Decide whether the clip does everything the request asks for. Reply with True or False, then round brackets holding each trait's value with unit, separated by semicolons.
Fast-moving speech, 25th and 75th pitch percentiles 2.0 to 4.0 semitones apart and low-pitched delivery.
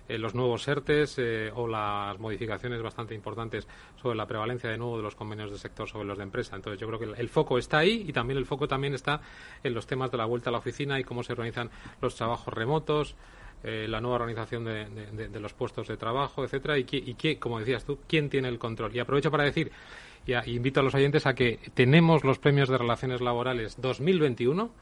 True (235 wpm; 3.4 semitones; 120 Hz)